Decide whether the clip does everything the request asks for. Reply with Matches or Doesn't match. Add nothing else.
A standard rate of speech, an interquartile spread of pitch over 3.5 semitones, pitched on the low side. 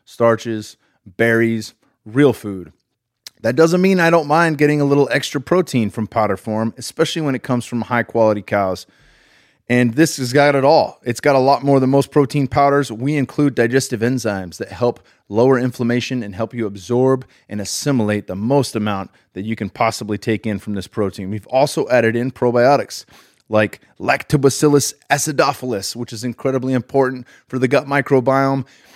Matches